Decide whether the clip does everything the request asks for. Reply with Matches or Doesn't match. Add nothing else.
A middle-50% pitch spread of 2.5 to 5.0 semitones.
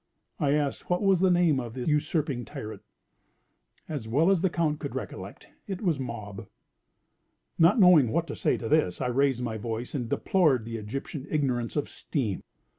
Doesn't match